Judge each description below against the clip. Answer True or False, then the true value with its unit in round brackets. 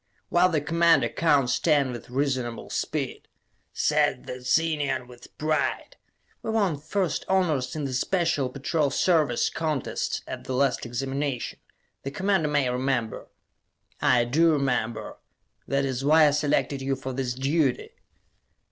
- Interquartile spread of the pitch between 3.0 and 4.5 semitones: True (3.7 semitones)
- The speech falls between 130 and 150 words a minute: True (140 wpm)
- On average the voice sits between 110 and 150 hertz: True (140 Hz)